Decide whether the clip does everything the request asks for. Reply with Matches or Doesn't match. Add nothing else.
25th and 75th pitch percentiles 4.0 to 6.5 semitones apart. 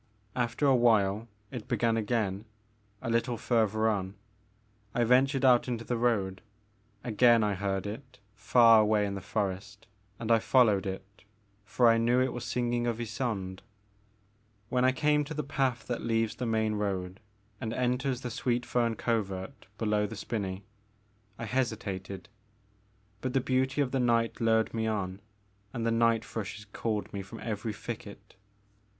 Doesn't match